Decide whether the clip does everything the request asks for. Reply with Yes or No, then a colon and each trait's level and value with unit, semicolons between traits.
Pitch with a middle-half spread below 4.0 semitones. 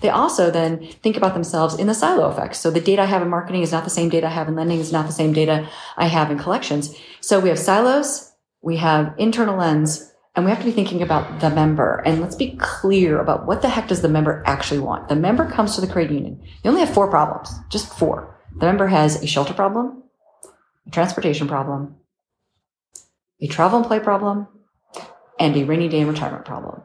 No: average, 4.3 semitones